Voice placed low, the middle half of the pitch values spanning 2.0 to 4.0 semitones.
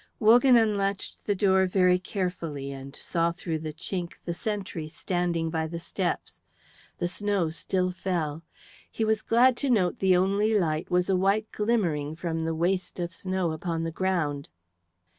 No: medium, 180 Hz; average, 3.3 semitones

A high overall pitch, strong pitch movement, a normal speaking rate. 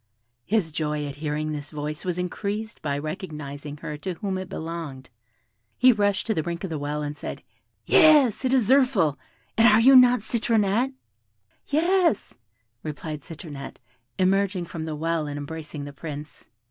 No: medium, 165 Hz; wide, 6.2 semitones; average, 160 wpm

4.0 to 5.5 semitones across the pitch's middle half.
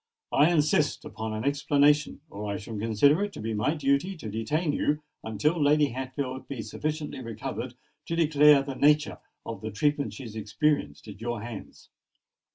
Yes: average, 5.0 semitones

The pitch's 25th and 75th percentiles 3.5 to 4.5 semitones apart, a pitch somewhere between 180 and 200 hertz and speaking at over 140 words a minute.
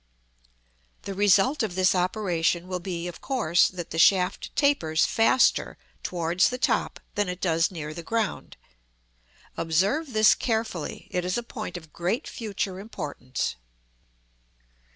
No: average, 4.2 semitones; medium, 185 Hz; slow, 135 wpm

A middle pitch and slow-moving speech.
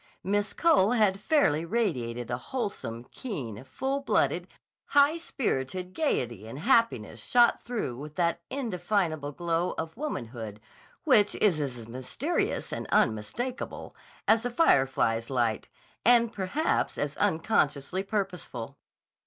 Yes: medium, 180 Hz; slow, 120 wpm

